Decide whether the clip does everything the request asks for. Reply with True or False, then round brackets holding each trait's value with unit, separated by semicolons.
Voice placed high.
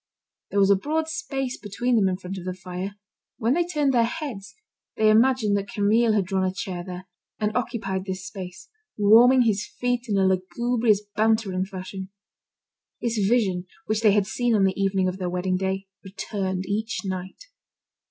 True (200 Hz)